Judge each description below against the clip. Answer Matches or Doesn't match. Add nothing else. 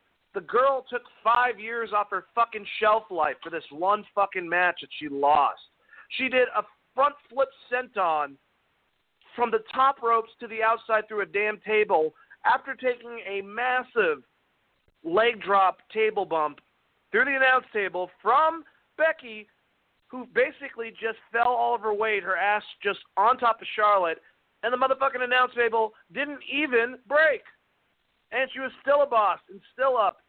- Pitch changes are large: Doesn't match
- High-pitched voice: Matches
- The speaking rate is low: Doesn't match